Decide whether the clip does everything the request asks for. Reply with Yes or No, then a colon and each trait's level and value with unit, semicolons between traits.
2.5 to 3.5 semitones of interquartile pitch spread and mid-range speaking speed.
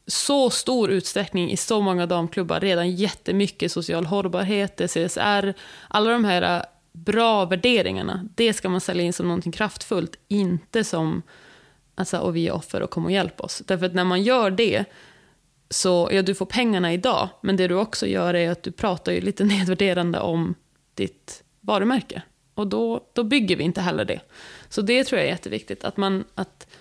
Yes: average, 3.0 semitones; average, 185 wpm